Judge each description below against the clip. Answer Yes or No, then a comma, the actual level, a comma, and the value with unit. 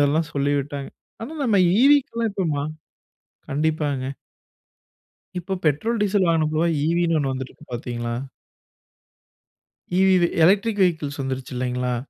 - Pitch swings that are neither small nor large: No, wide, 5.8 semitones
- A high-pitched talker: No, medium, 155 Hz